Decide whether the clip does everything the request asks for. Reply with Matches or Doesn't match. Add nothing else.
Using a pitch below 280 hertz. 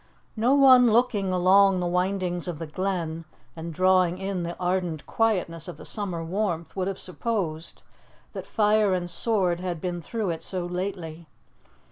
Matches